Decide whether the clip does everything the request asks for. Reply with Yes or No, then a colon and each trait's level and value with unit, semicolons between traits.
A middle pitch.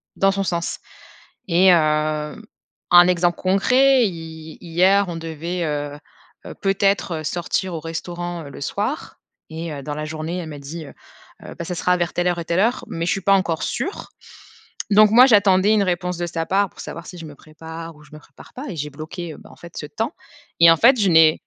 Yes: medium, 170 Hz